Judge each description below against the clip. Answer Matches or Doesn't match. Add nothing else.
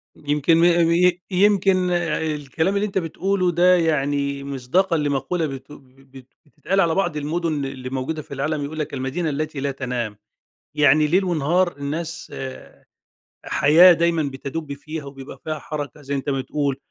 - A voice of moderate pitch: Matches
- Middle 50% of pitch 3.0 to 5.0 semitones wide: Matches